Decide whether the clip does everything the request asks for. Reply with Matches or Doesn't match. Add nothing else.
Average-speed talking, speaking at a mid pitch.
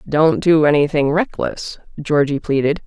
Doesn't match